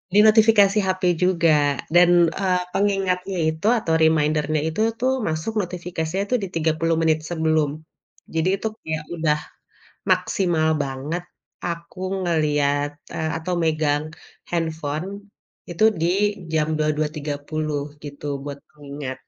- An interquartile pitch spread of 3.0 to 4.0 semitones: Yes, average, 3.4 semitones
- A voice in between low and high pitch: Yes, medium, 160 Hz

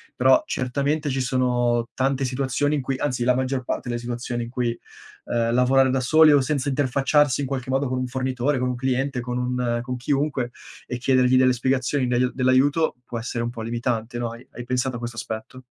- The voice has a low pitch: Yes, low, 125 Hz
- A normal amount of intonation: No, narrow, 1.6 semitones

